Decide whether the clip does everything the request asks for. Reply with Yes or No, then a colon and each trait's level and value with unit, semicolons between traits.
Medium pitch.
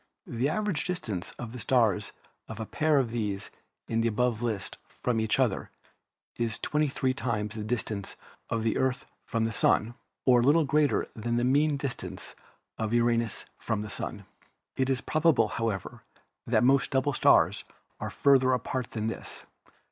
No: low, 120 Hz